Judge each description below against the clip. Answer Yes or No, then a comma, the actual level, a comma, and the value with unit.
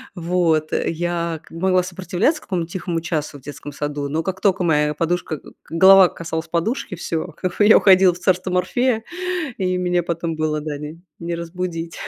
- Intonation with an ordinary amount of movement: No, narrow, 2.2 semitones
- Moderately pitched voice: Yes, medium, 170 Hz